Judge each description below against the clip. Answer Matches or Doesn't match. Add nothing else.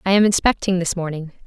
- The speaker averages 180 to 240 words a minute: Matches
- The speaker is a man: Doesn't match